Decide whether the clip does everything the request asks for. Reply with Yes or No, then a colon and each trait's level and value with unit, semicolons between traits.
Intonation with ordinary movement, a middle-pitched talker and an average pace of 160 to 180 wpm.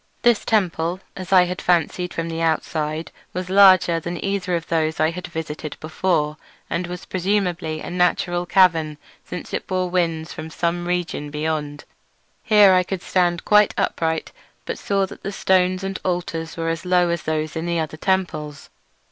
No: narrow, 2.3 semitones; medium, 175 Hz; average, 175 wpm